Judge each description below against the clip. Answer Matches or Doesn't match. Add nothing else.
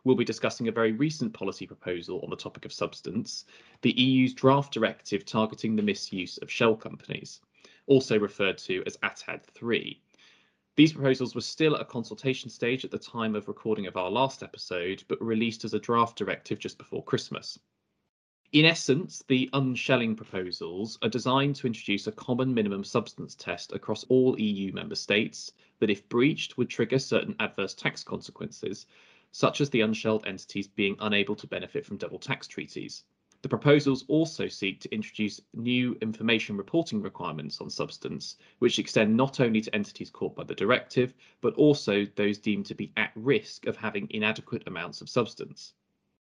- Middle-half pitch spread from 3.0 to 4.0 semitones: Matches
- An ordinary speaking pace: Matches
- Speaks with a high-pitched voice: Doesn't match